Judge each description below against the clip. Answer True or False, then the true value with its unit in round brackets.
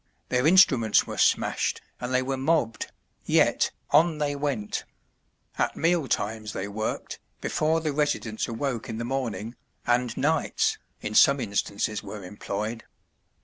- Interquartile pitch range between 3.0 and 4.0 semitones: False (5.0 semitones)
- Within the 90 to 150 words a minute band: True (140 wpm)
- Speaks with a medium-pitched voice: False (125 Hz)